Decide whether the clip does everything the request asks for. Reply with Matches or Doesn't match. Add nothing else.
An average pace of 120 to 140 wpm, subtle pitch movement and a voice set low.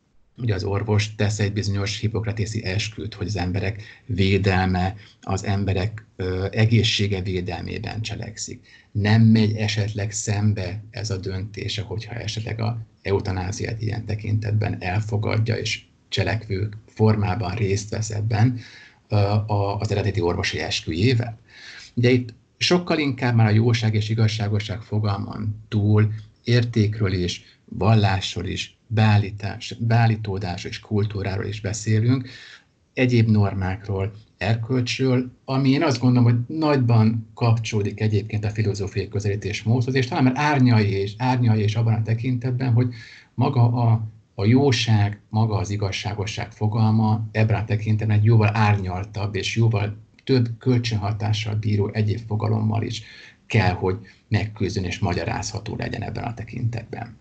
Matches